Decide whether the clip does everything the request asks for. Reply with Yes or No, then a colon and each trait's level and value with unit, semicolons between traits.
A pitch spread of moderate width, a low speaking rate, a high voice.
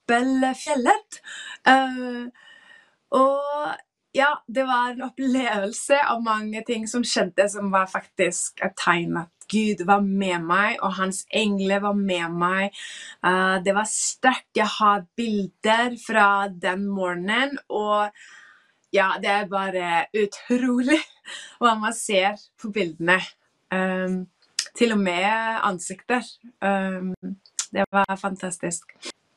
Yes: average, 4.2 semitones; slow, 120 wpm; high, 205 Hz